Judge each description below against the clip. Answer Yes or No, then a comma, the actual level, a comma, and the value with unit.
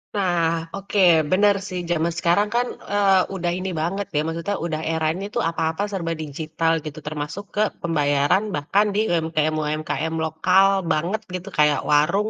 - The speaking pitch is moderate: Yes, medium, 170 Hz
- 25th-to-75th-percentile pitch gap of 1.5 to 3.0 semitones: No, average, 3.8 semitones